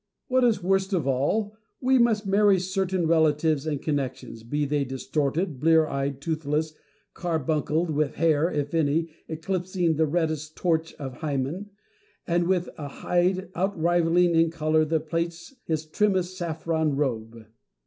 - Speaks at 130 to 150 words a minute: Yes, average, 140 wpm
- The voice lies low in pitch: No, medium, 160 Hz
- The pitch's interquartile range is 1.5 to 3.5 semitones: Yes, average, 3.1 semitones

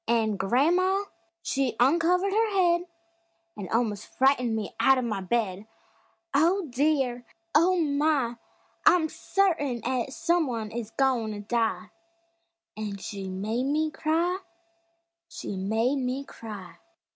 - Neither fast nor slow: No, slow, 125 wpm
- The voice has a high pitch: Yes, very high, 260 Hz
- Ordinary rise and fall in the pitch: No, wide, 6.5 semitones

